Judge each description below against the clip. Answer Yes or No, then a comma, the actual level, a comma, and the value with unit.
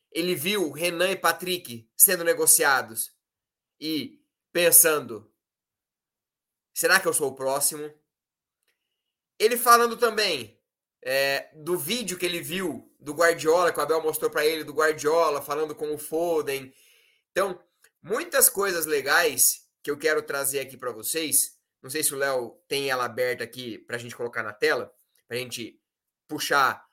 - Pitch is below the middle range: No, medium, 160 Hz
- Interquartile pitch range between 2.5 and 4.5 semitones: No, wide, 5.6 semitones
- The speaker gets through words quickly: No, average, 150 wpm